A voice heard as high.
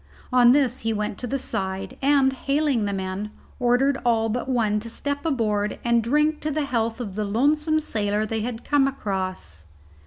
Yes: high, 235 Hz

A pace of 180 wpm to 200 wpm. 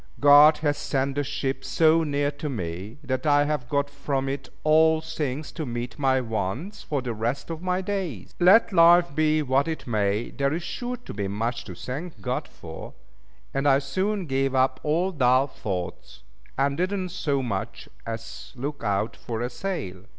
Yes: average, 185 wpm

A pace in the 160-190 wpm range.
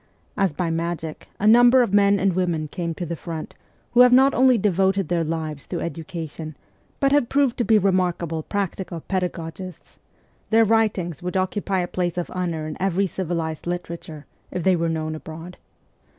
Yes: average, 175 wpm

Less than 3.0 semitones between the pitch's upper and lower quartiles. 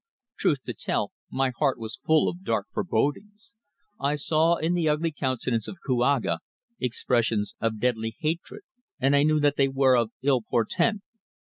No: average, 4.8 semitones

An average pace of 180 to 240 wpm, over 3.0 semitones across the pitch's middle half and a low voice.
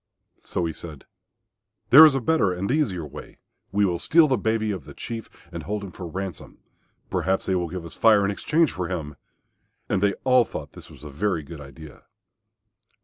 Yes: average, 200 wpm; average, 5.0 semitones; very low, 95 Hz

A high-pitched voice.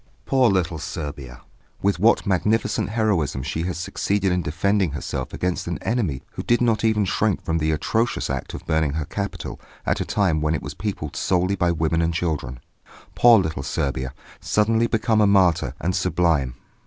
No: very low, 90 Hz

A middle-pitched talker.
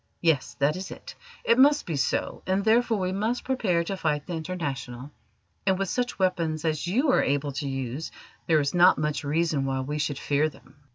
Yes: medium, 160 Hz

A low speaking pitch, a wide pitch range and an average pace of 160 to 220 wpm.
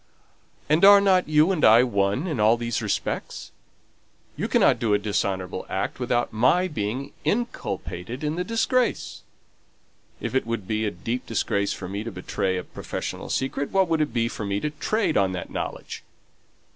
Yes: low, 120 Hz; wide, 7.3 semitones; average, 175 wpm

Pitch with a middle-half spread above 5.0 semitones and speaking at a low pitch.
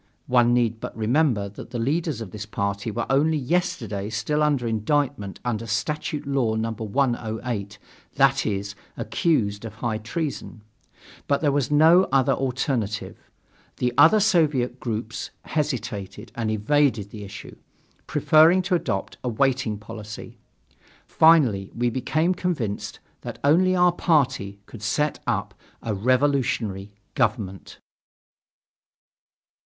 Yes: wide, 5.4 semitones; low, 120 Hz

